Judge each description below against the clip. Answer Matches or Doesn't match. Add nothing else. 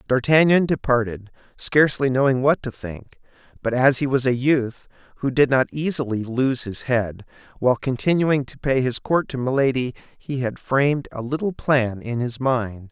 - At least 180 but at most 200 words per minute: Doesn't match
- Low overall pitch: Matches